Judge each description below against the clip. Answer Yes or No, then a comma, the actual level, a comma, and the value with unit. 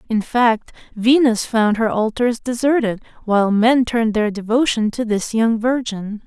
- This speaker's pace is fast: No, average, 155 wpm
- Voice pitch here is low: No, high, 225 Hz